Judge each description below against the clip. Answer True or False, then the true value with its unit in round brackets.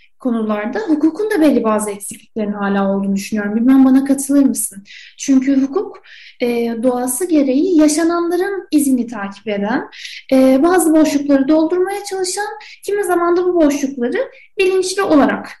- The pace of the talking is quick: False (130 wpm)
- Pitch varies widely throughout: True (7.5 semitones)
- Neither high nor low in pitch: False (285 Hz)